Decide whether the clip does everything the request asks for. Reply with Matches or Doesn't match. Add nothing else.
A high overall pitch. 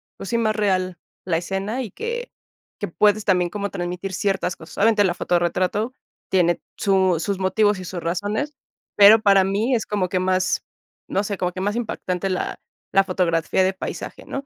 Matches